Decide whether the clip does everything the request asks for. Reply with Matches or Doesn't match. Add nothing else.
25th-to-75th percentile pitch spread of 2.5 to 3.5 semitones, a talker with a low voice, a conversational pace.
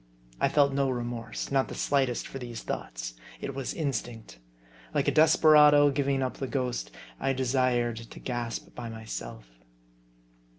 Matches